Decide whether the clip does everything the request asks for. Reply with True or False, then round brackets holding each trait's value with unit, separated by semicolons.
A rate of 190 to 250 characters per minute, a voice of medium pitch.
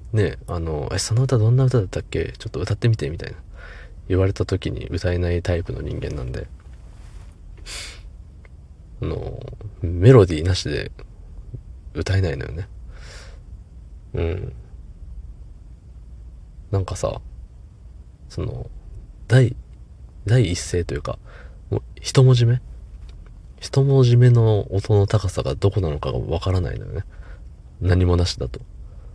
False (240 characters per minute; 90 Hz)